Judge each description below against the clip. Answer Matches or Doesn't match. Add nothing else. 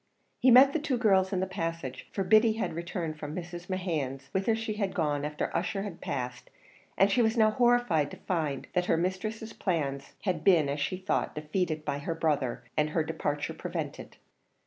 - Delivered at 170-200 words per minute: Matches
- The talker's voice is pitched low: Doesn't match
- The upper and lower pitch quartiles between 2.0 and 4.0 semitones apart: Doesn't match